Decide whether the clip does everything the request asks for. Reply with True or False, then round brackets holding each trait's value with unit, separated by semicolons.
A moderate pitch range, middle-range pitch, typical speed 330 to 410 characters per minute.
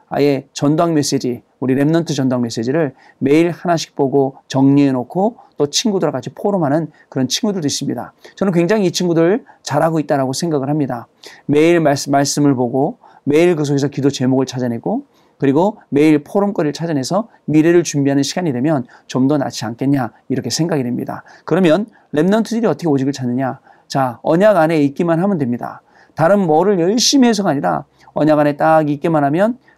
True (3.8 semitones; 150 Hz; 385 characters per minute)